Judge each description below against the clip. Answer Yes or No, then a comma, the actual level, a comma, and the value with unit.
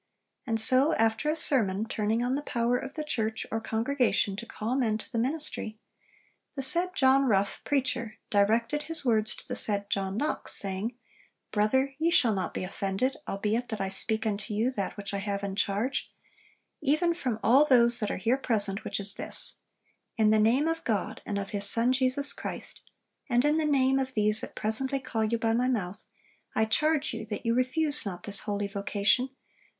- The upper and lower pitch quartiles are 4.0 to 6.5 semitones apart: Yes, average, 4.3 semitones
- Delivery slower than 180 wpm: No, average, 195 wpm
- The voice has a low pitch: No, high, 230 Hz